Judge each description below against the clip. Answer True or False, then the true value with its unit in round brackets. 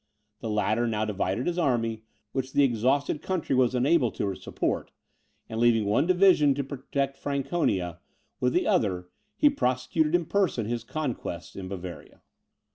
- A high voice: False (125 Hz)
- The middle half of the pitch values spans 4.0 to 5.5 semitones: True (5.1 semitones)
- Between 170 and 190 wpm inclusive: False (150 wpm)